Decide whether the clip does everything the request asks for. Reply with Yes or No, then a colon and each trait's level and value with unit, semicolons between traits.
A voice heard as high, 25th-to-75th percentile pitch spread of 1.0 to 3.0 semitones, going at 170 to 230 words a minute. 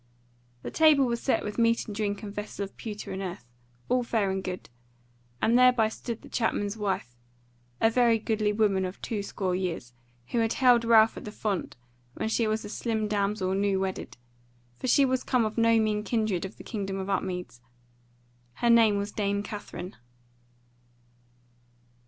Yes: high, 210 Hz; average, 2.7 semitones; average, 175 wpm